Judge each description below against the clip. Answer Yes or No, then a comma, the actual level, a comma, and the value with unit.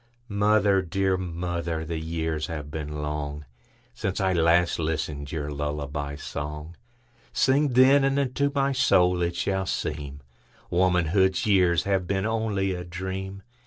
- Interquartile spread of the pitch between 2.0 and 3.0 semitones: No, average, 4.5 semitones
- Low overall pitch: Yes, very low, 90 Hz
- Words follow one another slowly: Yes, slow, 125 wpm